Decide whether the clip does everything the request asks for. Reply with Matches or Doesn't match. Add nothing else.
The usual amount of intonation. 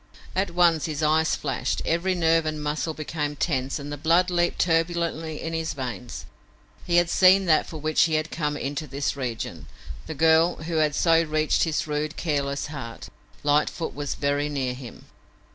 Doesn't match